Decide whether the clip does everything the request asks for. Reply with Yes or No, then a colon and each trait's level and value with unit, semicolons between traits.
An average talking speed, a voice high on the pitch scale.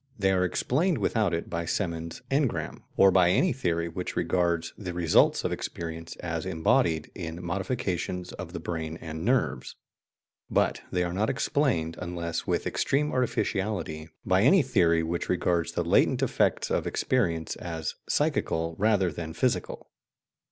No: average, 150 wpm; very low, 90 Hz